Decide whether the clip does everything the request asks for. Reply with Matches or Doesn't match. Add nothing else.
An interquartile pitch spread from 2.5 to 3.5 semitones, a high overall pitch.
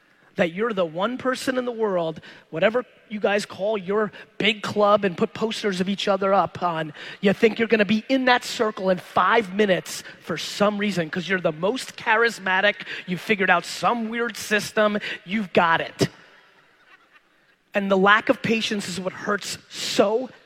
Matches